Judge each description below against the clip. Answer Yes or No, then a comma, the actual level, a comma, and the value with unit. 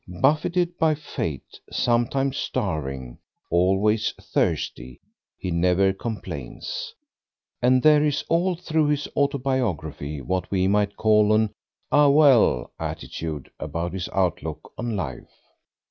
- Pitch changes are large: Yes, wide, 8.3 semitones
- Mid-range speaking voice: No, low, 105 Hz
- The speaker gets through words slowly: Yes, slow, 115 wpm